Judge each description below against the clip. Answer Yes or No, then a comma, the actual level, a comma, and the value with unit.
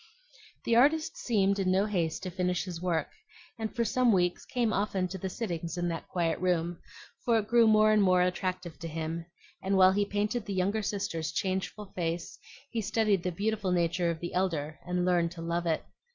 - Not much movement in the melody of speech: No, average, 3.3 semitones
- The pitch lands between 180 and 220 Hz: Yes, medium, 185 Hz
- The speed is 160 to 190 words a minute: No, average, 200 wpm